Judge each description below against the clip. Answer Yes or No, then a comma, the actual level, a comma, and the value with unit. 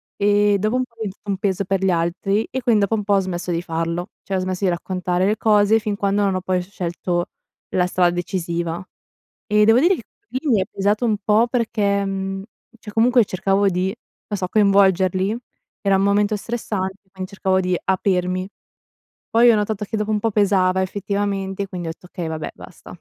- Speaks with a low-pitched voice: No, high, 195 Hz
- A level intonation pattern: Yes, narrow, 2.2 semitones